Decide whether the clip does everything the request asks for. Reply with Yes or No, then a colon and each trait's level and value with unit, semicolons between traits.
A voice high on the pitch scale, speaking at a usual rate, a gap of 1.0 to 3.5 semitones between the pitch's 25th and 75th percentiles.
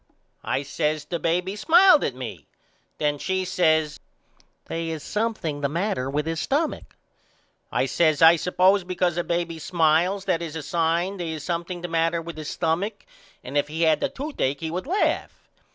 No: medium, 165 Hz; average, 180 wpm; average, 2.8 semitones